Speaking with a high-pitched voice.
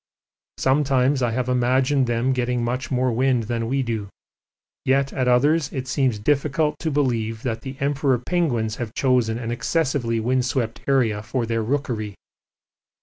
No: low, 125 Hz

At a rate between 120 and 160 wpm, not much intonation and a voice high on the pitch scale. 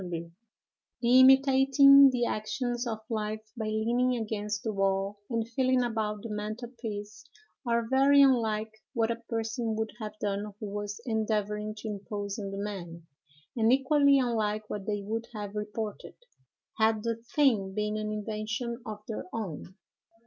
Yes: average, 150 wpm; narrow, 2.2 semitones; high, 220 Hz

